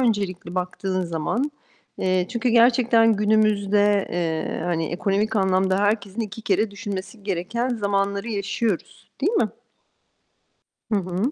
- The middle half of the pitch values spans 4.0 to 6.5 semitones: No, average, 3.1 semitones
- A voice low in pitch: No, high, 200 Hz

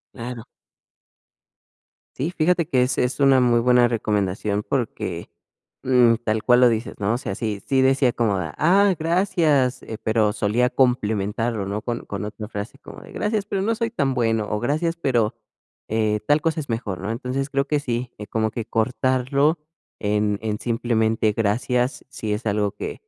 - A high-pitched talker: No, low, 120 Hz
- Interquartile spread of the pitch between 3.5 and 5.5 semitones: Yes, average, 4.1 semitones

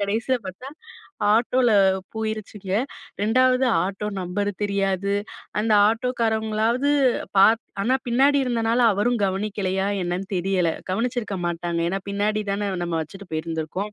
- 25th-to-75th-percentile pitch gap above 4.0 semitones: No, average, 3.3 semitones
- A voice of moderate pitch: No, high, 210 Hz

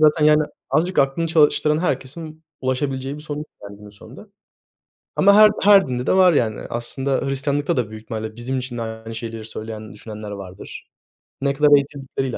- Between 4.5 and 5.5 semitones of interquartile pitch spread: Yes, average, 5.2 semitones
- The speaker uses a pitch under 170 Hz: Yes, low, 135 Hz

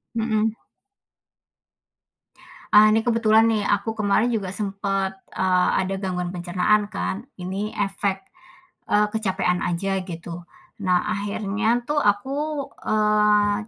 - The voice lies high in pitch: Yes, high, 205 Hz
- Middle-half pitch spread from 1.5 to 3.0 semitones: Yes, narrow, 2.4 semitones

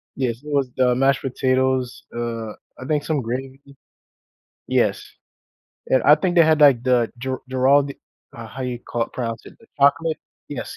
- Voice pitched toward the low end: Yes, low, 130 Hz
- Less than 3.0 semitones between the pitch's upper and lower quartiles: Yes, narrow, 2.5 semitones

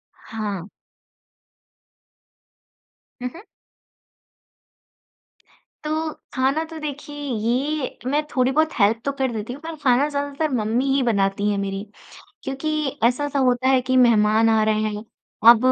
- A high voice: Yes, very high, 255 Hz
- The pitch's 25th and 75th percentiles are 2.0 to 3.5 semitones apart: No, average, 4.7 semitones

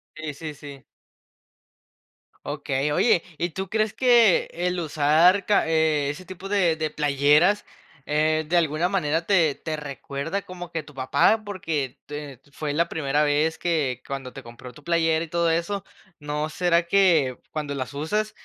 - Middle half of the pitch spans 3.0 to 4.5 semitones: Yes, average, 3.3 semitones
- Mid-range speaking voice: Yes, medium, 160 Hz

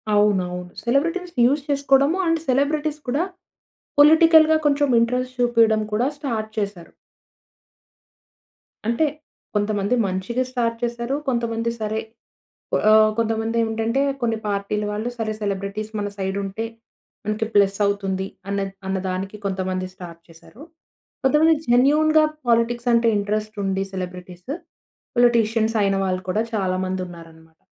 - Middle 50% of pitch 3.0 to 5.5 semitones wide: Yes, average, 4.4 semitones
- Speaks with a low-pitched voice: No, high, 220 Hz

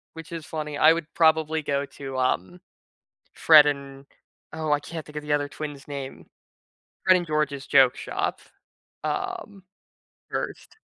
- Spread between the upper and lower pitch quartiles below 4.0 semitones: Yes, narrow, 2.4 semitones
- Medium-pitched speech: Yes, medium, 150 Hz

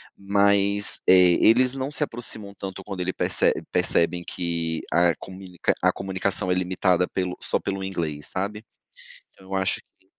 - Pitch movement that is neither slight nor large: No, narrow, 1.9 semitones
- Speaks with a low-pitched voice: Yes, very low, 95 Hz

